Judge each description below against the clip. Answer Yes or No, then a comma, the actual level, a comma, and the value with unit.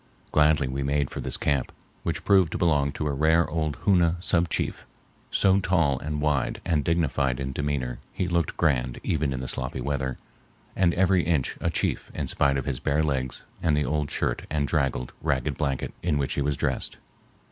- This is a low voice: Yes, very low, 75 Hz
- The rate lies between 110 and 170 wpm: No, average, 195 wpm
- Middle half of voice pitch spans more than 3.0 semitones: Yes, average, 3.5 semitones